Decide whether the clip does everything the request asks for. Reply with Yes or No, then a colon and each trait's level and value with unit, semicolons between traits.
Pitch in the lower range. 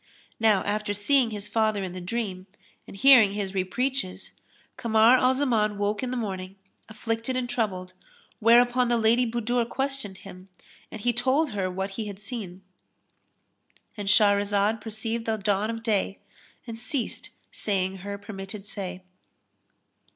No: high, 215 Hz